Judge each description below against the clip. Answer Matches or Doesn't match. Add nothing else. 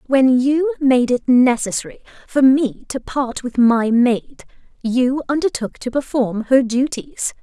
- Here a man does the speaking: Doesn't match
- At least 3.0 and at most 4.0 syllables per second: Matches